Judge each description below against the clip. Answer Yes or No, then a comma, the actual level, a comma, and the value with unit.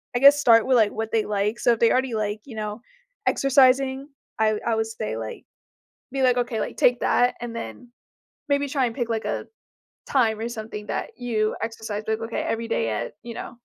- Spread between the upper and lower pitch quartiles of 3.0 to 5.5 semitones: No, narrow, 2.5 semitones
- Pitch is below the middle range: No, high, 230 Hz